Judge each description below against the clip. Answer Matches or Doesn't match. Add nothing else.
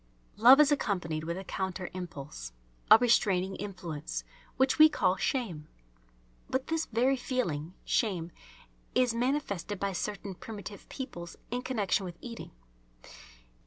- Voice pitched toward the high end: Matches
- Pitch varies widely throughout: Matches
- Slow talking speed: Matches